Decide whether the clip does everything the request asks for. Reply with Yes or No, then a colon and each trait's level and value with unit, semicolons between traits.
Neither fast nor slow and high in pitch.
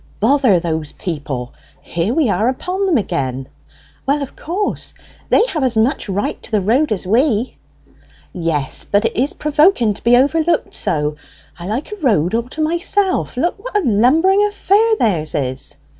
Yes: average, 170 wpm; high, 240 Hz